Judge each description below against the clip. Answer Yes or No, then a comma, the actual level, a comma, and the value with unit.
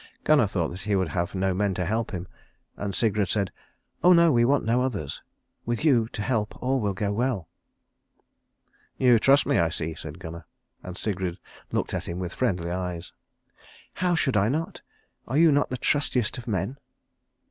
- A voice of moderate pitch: No, low, 105 Hz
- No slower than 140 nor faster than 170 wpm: No, average, 185 wpm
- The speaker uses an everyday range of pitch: No, wide, 5.7 semitones